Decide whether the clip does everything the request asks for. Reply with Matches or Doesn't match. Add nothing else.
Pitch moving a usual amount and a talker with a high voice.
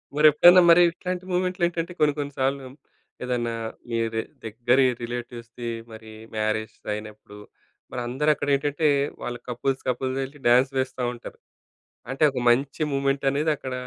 Doesn't match